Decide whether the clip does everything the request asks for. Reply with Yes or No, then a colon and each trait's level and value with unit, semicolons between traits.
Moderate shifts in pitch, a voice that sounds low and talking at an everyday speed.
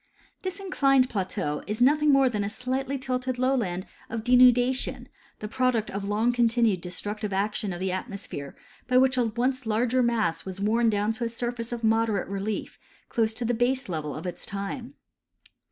No: average, 3.8 semitones; high, 230 Hz; average, 170 wpm